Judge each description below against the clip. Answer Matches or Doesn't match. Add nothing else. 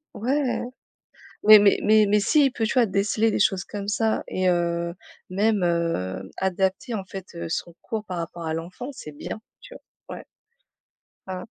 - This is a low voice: Doesn't match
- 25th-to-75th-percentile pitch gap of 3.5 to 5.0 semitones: Matches